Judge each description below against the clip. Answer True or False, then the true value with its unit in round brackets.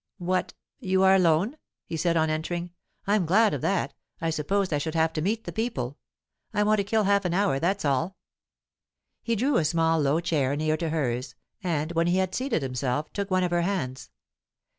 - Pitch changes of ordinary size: True (4.1 semitones)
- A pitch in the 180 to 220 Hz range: False (170 Hz)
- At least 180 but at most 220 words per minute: True (205 wpm)